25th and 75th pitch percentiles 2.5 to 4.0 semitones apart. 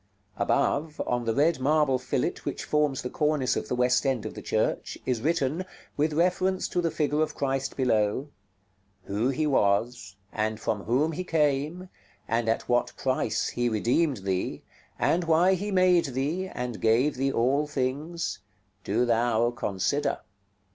No: average, 4.5 semitones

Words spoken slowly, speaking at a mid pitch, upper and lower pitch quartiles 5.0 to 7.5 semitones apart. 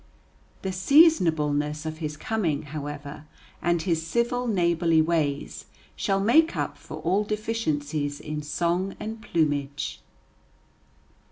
Yes: slow, 110 wpm; medium, 165 Hz; average, 5.3 semitones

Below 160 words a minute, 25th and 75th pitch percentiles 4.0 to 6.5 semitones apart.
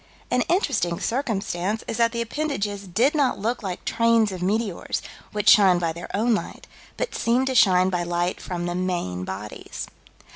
No: average, 175 wpm; average, 4.8 semitones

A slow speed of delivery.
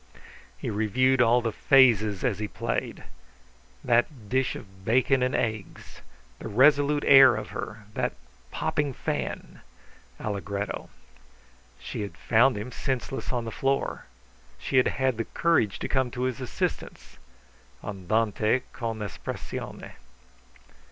Yes: slow, 125 wpm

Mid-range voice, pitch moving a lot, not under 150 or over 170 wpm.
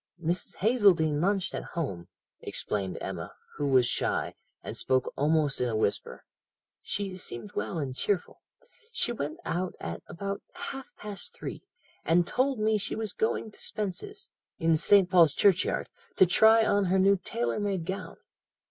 Yes: medium, 180 Hz; wide, 5.9 semitones; average, 155 wpm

